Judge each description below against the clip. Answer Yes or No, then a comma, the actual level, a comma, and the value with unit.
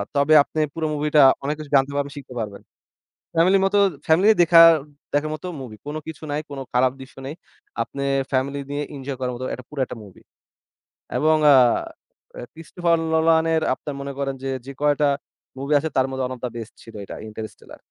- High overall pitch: No, medium, 140 Hz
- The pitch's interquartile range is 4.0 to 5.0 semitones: No, average, 3.1 semitones